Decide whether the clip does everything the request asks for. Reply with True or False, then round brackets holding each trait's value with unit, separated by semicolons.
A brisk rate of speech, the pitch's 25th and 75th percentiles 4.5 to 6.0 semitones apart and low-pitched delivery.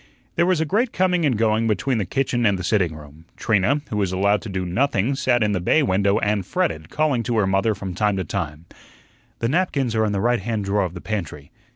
True (240 wpm; 4.8 semitones; 105 Hz)